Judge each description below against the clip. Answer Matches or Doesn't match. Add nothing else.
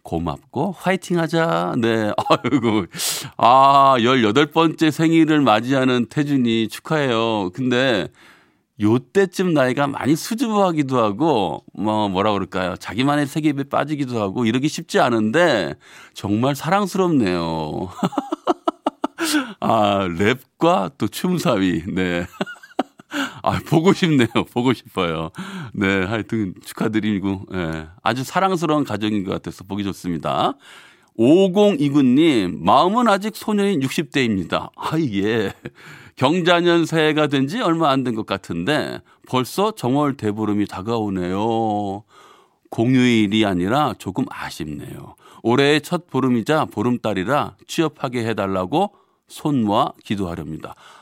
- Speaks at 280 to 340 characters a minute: Doesn't match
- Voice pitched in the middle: Doesn't match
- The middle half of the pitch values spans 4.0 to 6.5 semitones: Doesn't match